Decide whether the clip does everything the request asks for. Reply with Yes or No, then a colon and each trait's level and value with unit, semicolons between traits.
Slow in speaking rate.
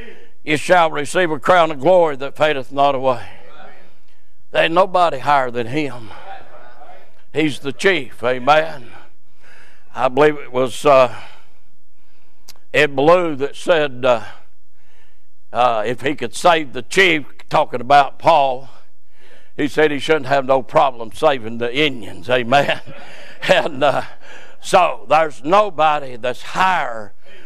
Yes: slow, 130 wpm